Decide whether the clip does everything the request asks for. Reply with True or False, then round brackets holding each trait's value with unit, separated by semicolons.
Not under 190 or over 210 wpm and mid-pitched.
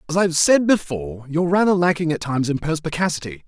True (205 wpm; 160 Hz)